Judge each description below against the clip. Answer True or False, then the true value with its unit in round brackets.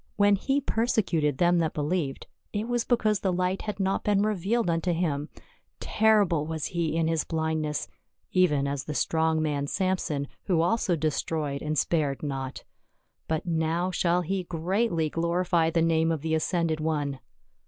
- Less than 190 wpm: True (160 wpm)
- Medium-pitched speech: True (165 Hz)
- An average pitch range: True (3.2 semitones)